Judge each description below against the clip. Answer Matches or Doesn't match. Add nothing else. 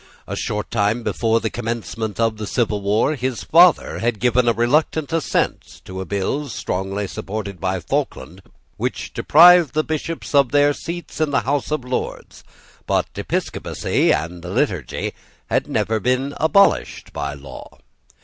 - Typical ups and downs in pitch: Doesn't match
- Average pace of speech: Matches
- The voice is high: Doesn't match